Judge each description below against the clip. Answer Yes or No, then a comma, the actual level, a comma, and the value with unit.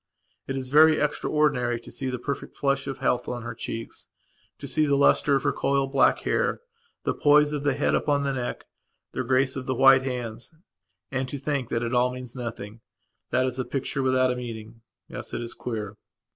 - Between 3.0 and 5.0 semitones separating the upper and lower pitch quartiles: No, narrow, 2.4 semitones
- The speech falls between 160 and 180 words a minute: No, average, 200 wpm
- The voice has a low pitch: Yes, low, 130 Hz